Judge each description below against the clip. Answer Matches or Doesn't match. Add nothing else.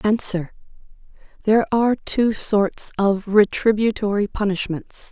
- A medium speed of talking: Doesn't match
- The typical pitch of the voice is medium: Doesn't match